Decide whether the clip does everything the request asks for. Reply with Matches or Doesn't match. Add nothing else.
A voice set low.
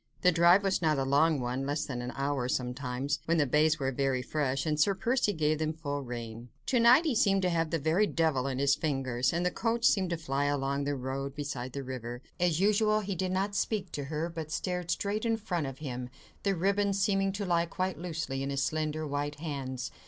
Doesn't match